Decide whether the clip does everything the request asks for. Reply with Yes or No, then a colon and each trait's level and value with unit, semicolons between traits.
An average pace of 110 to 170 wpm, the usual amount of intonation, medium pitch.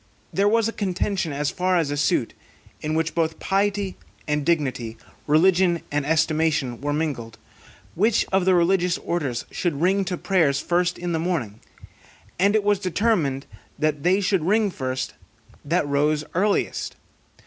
Yes: average, 155 wpm; average, 4.3 semitones; medium, 170 Hz